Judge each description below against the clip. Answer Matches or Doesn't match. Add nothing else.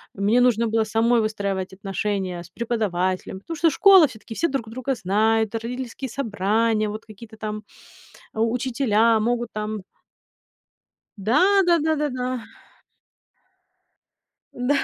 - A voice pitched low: Doesn't match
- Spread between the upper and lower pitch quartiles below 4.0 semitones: Matches